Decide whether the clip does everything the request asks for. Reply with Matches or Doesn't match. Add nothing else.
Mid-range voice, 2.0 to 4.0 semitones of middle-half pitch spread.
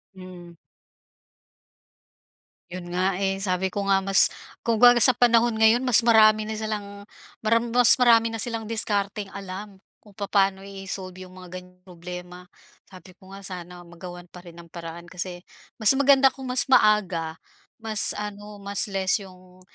Doesn't match